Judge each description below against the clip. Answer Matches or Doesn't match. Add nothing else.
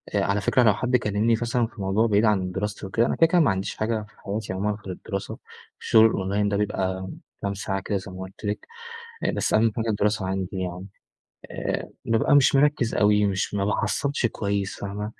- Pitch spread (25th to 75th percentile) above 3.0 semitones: Doesn't match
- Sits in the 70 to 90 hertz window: Doesn't match